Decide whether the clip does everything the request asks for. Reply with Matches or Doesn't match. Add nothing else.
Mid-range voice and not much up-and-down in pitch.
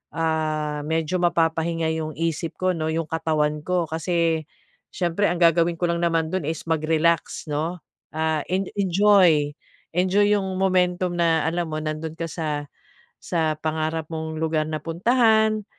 Matches